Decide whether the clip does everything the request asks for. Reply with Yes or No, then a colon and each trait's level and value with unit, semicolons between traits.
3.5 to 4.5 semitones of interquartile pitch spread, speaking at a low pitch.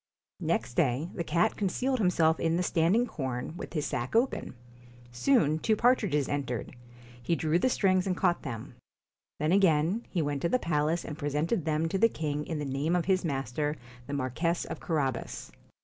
No: average, 4.0 semitones; medium, 160 Hz